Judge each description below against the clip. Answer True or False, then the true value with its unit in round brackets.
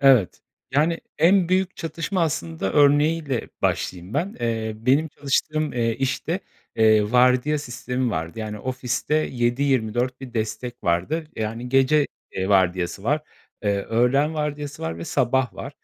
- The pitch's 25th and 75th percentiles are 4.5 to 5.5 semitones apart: True (5.2 semitones)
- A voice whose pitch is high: False (125 Hz)